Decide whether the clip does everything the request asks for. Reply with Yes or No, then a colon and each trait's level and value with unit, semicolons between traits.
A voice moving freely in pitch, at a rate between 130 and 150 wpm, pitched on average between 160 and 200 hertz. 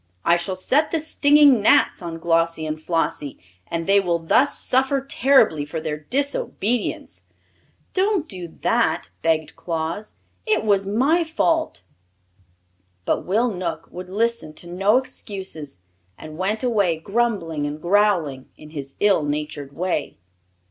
Yes: wide, 6.9 semitones; slow, 135 wpm; medium, 185 Hz